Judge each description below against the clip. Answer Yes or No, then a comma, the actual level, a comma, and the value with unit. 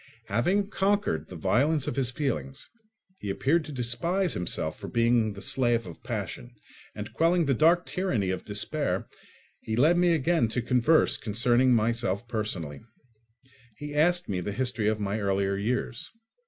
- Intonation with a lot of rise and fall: Yes, wide, 7.0 semitones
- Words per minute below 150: No, average, 155 wpm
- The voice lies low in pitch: Yes, low, 120 Hz